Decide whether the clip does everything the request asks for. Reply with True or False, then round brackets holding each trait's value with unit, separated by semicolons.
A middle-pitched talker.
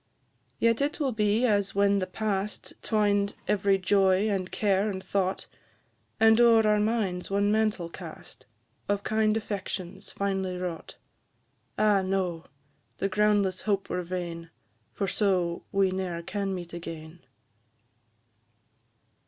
False (195 Hz)